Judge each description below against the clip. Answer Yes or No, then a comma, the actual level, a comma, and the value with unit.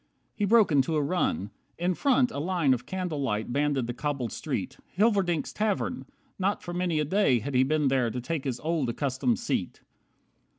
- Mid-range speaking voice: Yes, medium, 155 Hz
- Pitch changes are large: Yes, wide, 6.0 semitones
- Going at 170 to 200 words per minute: Yes, average, 185 wpm